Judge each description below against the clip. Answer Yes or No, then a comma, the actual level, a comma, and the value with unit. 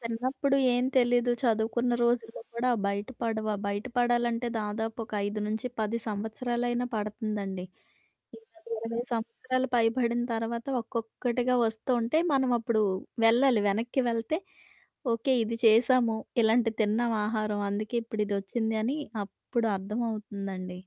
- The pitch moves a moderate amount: No, narrow, 2.0 semitones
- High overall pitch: Yes, high, 230 Hz